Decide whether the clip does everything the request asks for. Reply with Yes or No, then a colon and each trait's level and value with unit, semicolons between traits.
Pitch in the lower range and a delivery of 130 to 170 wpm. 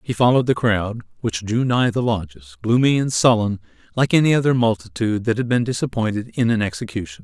No: low, 115 Hz; average, 190 wpm